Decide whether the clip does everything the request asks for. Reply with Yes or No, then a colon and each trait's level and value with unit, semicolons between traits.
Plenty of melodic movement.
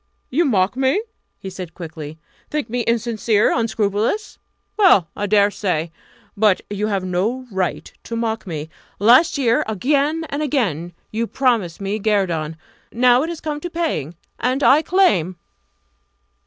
Yes: wide, 6.0 semitones